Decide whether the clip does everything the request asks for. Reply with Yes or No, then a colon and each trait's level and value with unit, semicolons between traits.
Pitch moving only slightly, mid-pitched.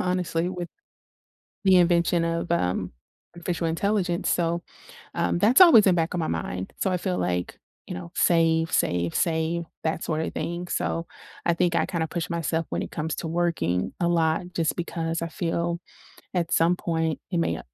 Yes: narrow, 1.4 semitones; medium, 170 Hz